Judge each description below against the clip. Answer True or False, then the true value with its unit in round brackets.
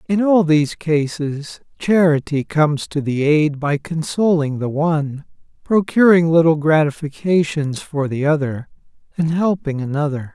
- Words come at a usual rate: False (130 wpm)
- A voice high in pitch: False (155 Hz)